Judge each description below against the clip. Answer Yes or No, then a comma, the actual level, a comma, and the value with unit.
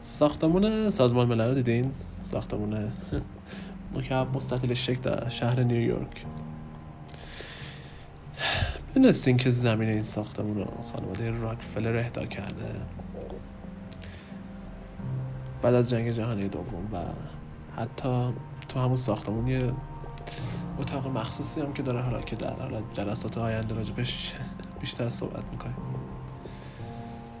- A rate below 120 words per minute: Yes, slow, 105 wpm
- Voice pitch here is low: Yes, low, 115 Hz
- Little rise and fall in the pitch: No, average, 3.9 semitones